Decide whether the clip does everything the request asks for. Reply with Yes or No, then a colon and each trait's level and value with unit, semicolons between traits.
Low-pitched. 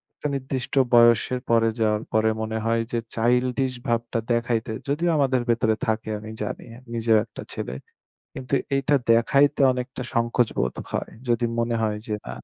Yes: low, 115 Hz